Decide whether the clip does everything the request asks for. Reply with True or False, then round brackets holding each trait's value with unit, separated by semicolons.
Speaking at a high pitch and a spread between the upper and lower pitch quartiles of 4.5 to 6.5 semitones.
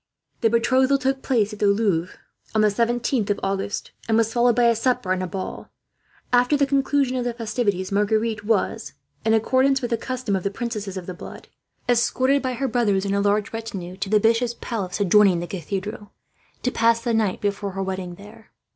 False (220 Hz; 3.4 semitones)